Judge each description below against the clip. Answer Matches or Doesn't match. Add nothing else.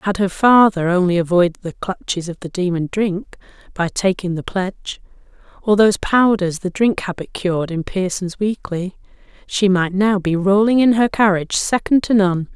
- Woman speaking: Matches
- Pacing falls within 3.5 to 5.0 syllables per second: Matches